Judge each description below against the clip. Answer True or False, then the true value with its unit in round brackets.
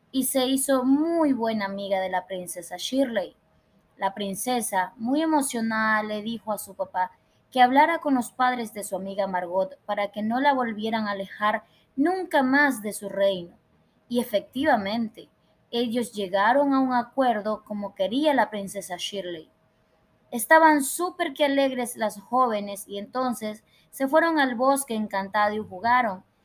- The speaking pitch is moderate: False (230 Hz)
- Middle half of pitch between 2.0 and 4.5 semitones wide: False (5.1 semitones)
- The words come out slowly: False (150 wpm)